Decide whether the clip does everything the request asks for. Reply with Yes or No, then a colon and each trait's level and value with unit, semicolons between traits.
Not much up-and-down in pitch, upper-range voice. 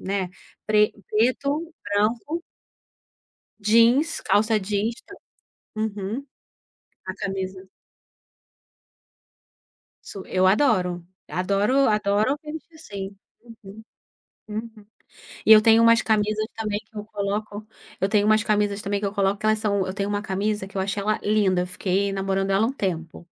Yes: narrow, 2.1 semitones; high, 210 Hz